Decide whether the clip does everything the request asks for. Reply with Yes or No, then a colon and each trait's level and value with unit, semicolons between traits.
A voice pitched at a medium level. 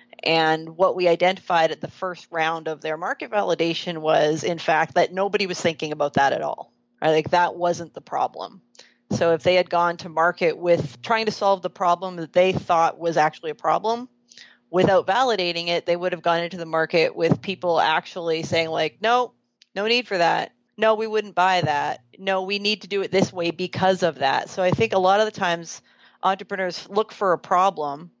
Yes: medium, 175 Hz